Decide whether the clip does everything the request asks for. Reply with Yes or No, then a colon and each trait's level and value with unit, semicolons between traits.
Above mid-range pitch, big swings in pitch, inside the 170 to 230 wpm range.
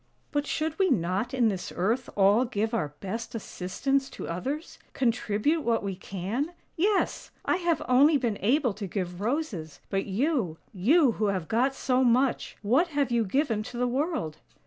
Yes: high, 235 Hz; wide, 6.2 semitones; average, 190 wpm